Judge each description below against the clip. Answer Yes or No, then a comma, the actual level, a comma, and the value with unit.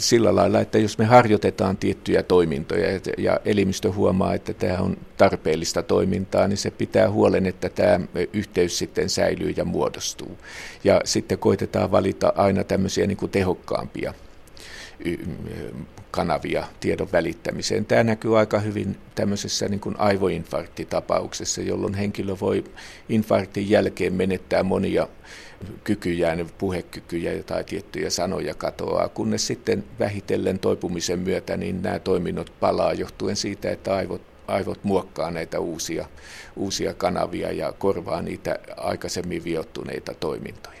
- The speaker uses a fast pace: No, average, 125 wpm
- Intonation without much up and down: Yes, narrow, 2.2 semitones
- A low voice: Yes, low, 100 Hz